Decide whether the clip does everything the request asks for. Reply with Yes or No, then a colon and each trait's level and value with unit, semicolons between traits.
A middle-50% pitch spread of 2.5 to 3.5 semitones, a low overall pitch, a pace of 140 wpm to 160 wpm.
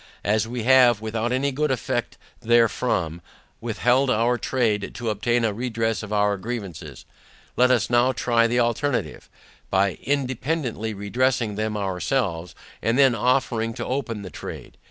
Yes: average, 3.2 semitones; low, 115 Hz; average, 145 wpm